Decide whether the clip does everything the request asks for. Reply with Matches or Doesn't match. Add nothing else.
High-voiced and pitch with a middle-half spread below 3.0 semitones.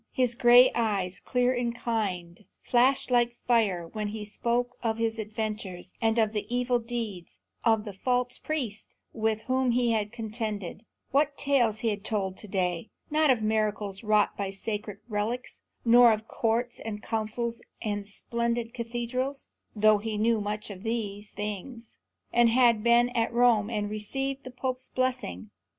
Matches